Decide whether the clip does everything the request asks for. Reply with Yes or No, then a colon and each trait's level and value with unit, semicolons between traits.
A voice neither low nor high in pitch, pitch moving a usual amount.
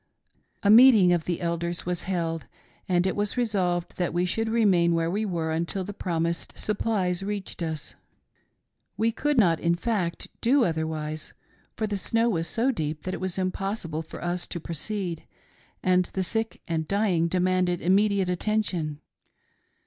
Yes: medium, 180 Hz; average, 3.6 semitones